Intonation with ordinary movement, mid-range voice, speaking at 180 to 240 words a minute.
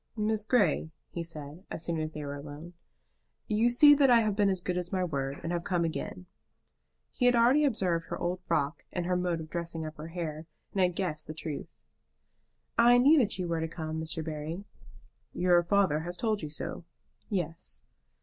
Yes: average, 4.2 semitones; medium, 175 Hz; average, 200 wpm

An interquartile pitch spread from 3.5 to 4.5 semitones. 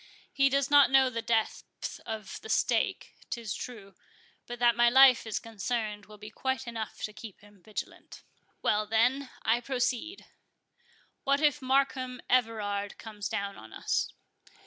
Yes: average, 3.8 semitones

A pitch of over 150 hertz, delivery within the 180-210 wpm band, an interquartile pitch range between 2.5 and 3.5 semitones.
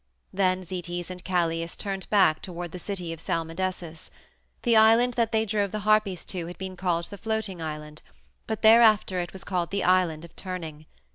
Yes: medium, 185 Hz; average, 185 wpm; average, 3.2 semitones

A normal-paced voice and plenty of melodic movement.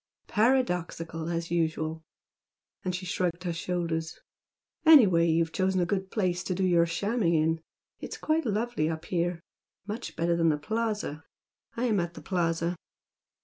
No: average, 150 wpm; average, 3.3 semitones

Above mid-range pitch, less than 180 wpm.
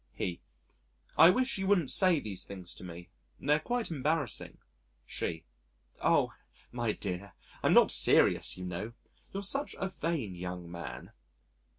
No: low, 120 Hz; average, 145 wpm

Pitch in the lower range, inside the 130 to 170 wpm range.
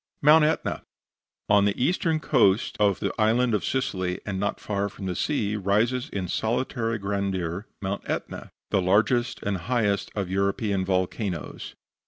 Yes: low, 100 Hz; average, 150 wpm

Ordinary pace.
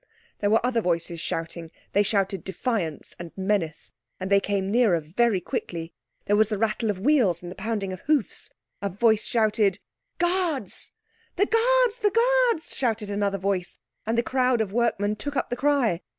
Yes: average, 175 wpm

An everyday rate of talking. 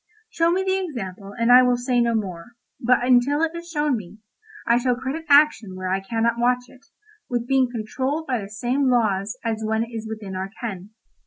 No: fast, 210 wpm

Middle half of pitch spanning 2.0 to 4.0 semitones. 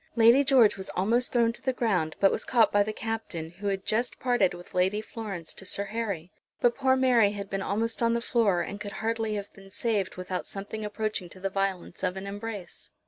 Yes: average, 3.0 semitones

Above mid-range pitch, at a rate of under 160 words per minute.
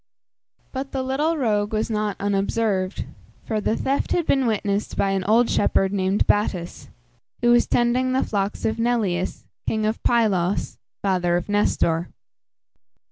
Yes: high, 210 Hz; average, 145 wpm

